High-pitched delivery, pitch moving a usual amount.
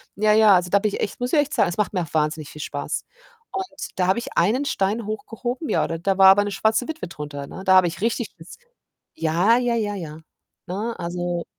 Yes: high, 195 Hz; average, 4.9 semitones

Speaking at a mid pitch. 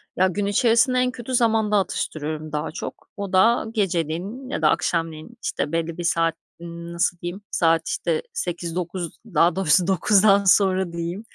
Yes: medium, 180 Hz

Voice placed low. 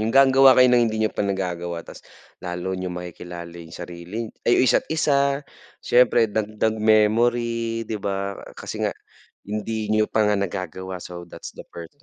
Yes: low, 105 Hz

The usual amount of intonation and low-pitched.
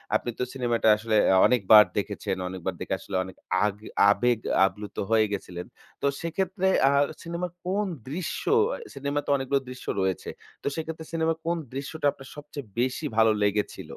No: wide, 7.2 semitones; low, 130 Hz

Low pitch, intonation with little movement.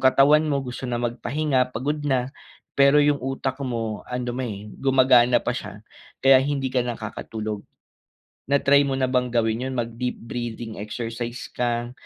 Yes: low, 125 Hz; narrow, 2.3 semitones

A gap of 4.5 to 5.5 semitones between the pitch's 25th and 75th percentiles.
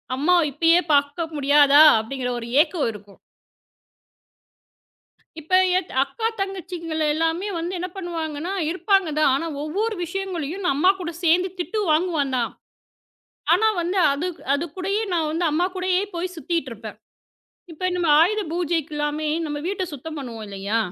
No: average, 3.8 semitones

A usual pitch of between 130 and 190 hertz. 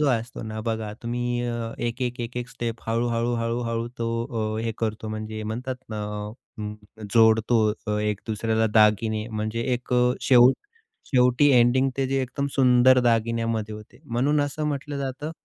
No: low, 120 Hz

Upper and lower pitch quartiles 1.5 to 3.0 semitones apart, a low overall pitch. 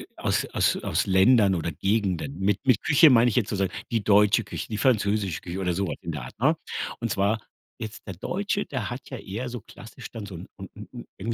No: average, 3.7 semitones; low, 105 Hz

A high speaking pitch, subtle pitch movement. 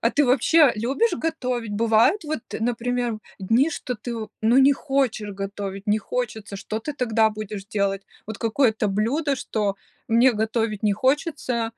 No: high, 230 Hz; average, 3.8 semitones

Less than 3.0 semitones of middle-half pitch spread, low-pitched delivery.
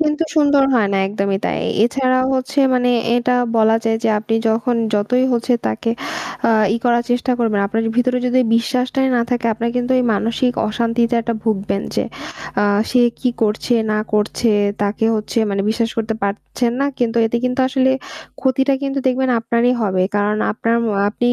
No: narrow, 2.6 semitones; high, 235 Hz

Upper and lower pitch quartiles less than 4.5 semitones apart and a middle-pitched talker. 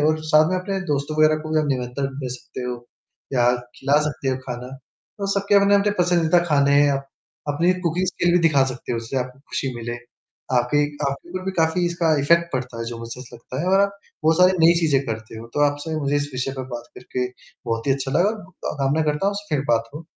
No: average, 5.1 semitones; medium, 145 Hz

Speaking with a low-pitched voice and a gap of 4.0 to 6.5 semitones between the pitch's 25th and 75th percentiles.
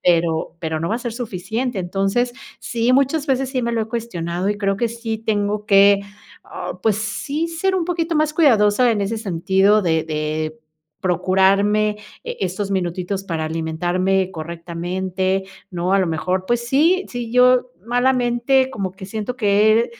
No: high, 205 Hz; average, 4.8 semitones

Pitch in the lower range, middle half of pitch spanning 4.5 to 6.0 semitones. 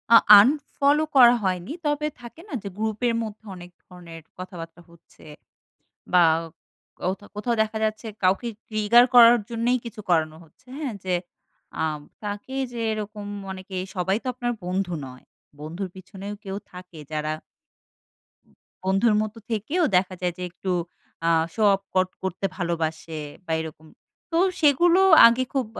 No: high, 205 Hz; average, 4.8 semitones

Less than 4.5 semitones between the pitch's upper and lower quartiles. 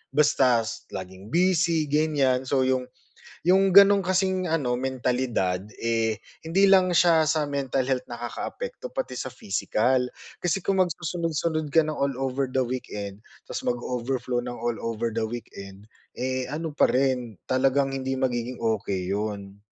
No: average, 5.3 semitones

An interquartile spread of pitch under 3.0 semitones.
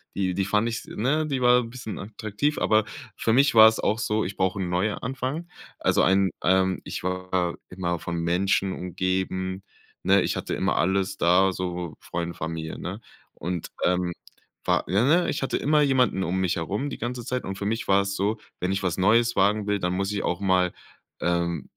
No: average, 3.6 semitones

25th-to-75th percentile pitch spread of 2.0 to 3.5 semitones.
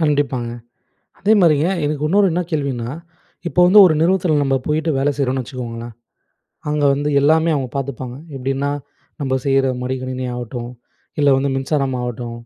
Yes: average, 3.1 semitones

